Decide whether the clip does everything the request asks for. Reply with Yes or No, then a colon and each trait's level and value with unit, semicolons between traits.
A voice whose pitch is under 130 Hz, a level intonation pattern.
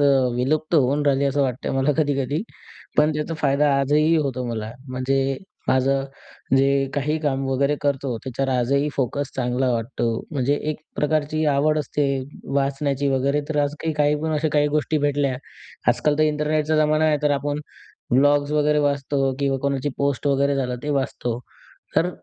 No: medium, 140 Hz; narrow, 1.8 semitones